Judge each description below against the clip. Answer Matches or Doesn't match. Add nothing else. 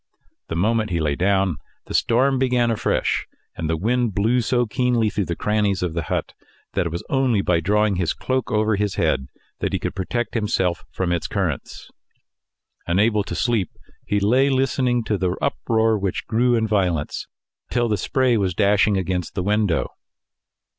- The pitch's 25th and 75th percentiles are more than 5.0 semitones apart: Doesn't match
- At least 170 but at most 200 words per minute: Matches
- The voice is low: Matches